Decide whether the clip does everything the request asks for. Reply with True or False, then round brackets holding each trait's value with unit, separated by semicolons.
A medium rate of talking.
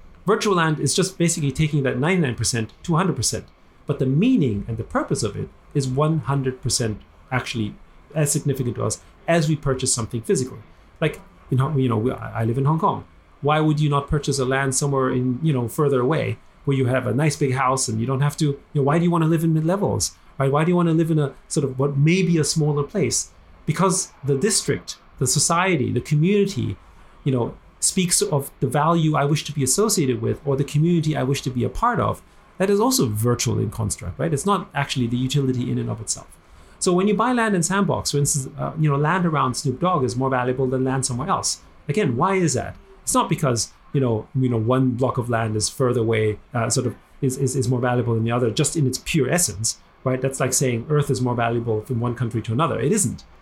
False (230 wpm)